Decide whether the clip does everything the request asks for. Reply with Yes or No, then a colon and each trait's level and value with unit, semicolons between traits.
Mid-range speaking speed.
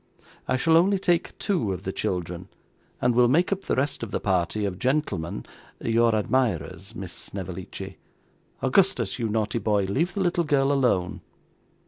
Yes: average, 160 wpm